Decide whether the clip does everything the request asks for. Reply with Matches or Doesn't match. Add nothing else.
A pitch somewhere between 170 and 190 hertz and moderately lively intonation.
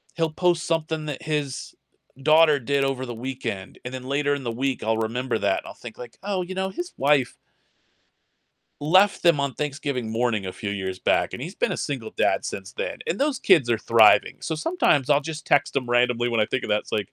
Doesn't match